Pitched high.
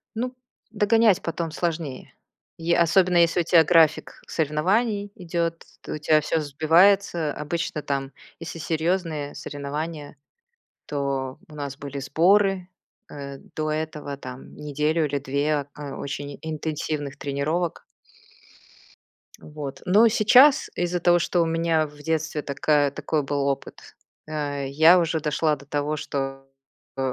No: medium, 155 Hz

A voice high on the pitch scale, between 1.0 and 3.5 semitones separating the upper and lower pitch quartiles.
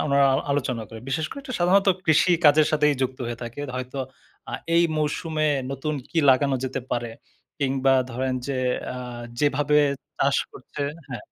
No: medium, 140 Hz; average, 2.8 semitones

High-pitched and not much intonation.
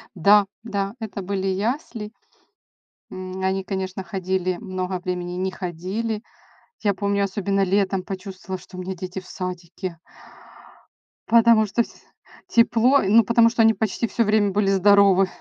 Yes: high, 195 Hz; narrow, 2.3 semitones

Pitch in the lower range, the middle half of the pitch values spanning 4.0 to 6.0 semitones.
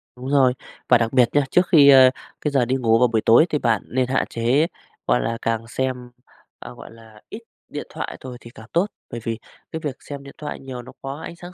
No: low, 130 Hz; average, 3.5 semitones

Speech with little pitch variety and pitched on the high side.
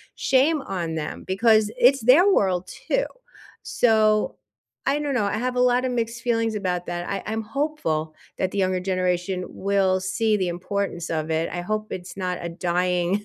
No: average, 4.4 semitones; high, 200 Hz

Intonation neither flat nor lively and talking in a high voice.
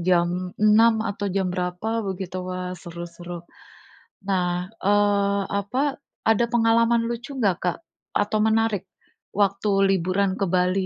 Yes: average, 3.1 semitones; high, 200 Hz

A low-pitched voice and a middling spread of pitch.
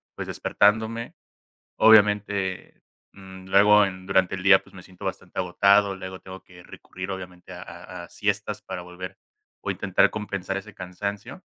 No: very low, 95 Hz; narrow, 1.9 semitones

